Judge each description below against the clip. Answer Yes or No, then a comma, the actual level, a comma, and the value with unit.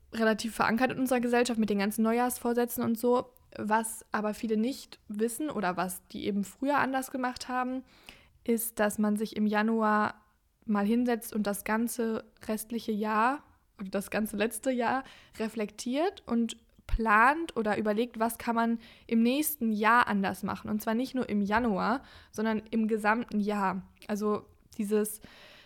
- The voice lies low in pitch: No, high, 225 Hz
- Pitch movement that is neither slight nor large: No, narrow, 2.3 semitones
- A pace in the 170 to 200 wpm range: No, average, 155 wpm